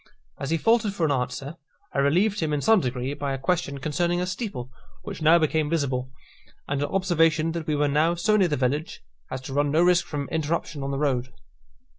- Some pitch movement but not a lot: Yes, average, 3.7 semitones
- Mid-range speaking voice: Yes, medium, 150 Hz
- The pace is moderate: No, fast, 215 wpm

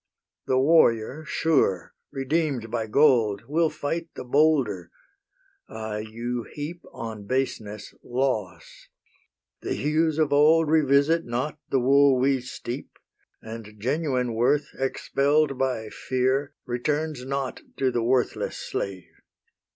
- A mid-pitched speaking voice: No, low, 130 Hz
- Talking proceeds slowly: Yes, slow, 115 wpm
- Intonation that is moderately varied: Yes, average, 4.2 semitones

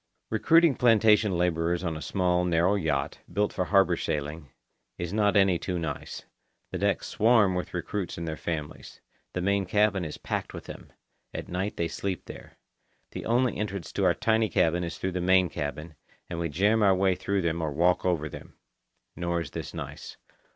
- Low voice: Yes, very low, 90 Hz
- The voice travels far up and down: No, average, 3.3 semitones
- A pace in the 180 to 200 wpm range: Yes, average, 185 wpm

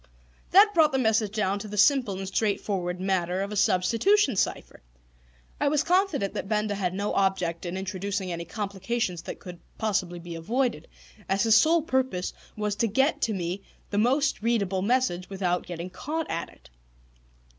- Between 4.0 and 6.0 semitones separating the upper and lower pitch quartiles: Yes, average, 4.5 semitones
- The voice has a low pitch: No, high, 200 Hz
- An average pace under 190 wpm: Yes, average, 170 wpm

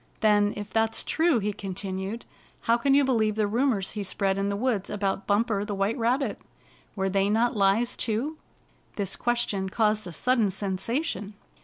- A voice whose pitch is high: Yes, high, 210 Hz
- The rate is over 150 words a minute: Yes, average, 180 wpm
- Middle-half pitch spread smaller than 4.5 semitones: Yes, average, 3.1 semitones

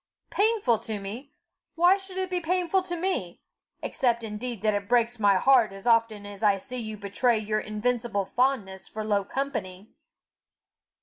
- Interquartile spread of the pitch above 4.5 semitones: Yes, average, 5.0 semitones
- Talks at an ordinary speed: Yes, average, 165 wpm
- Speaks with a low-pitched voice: No, high, 230 Hz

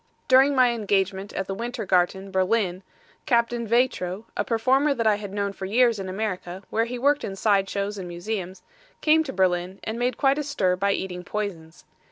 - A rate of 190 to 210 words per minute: Yes, average, 195 wpm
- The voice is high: Yes, high, 205 Hz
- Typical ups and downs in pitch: Yes, average, 4.0 semitones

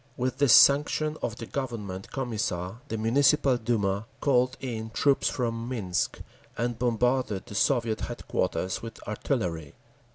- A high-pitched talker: No, low, 115 Hz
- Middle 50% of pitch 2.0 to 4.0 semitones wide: Yes, average, 3.3 semitones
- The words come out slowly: Yes, slow, 130 wpm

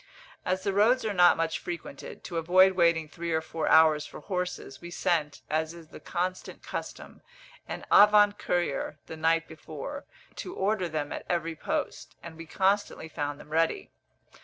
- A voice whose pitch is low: No, medium, 170 Hz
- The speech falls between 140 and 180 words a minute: Yes, average, 170 wpm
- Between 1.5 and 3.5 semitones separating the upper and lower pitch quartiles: Yes, average, 2.8 semitones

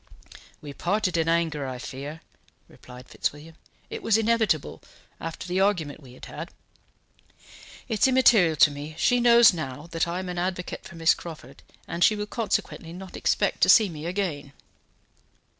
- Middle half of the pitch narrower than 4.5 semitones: No, average, 5.0 semitones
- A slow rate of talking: No, average, 165 wpm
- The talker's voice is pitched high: No, medium, 170 Hz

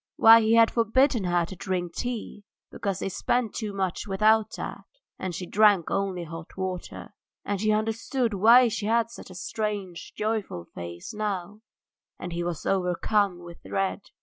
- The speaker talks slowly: No, average, 165 wpm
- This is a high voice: Yes, high, 200 Hz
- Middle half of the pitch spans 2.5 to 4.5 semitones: Yes, average, 3.6 semitones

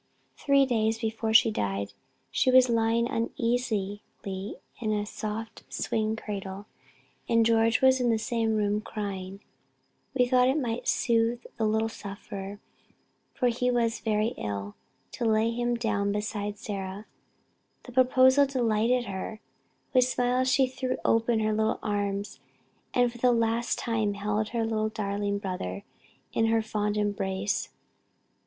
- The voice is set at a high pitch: Yes, high, 225 Hz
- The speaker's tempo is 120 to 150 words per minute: Yes, average, 140 wpm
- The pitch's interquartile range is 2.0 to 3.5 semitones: Yes, average, 2.7 semitones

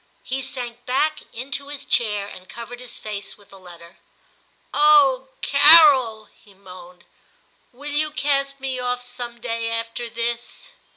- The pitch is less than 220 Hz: No, high, 245 Hz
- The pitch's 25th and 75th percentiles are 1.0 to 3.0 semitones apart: No, average, 4.0 semitones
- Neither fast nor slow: Yes, average, 155 wpm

